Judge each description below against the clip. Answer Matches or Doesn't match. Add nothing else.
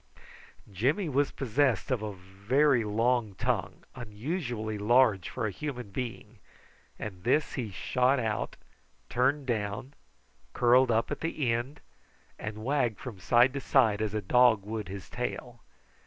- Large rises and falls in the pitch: Doesn't match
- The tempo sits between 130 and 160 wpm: Matches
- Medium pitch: Doesn't match